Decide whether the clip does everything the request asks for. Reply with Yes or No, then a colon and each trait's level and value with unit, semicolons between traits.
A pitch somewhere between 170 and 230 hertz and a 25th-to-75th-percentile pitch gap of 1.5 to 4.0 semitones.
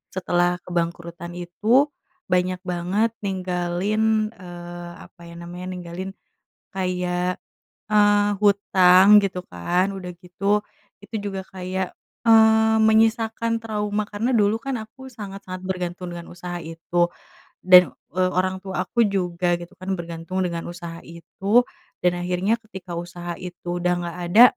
Yes: medium, 185 Hz; average, 2.9 semitones